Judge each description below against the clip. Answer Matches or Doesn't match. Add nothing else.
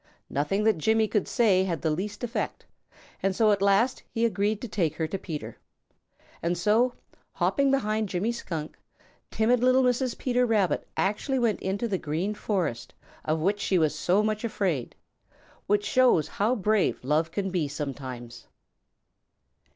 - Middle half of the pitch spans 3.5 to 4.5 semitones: Doesn't match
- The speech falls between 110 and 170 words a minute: Matches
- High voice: Matches